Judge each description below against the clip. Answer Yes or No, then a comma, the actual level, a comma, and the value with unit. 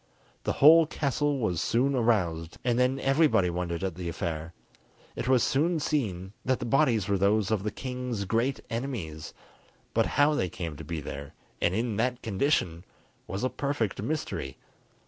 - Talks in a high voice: No, low, 110 Hz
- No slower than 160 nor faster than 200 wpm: Yes, average, 165 wpm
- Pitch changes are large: Yes, wide, 7.1 semitones